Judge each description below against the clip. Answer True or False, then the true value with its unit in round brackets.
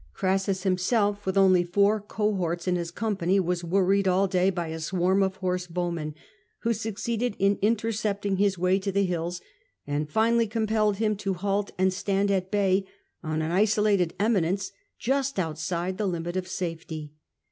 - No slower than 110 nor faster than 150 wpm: False (165 wpm)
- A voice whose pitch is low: False (190 Hz)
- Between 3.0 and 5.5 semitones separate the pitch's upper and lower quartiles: False (2.6 semitones)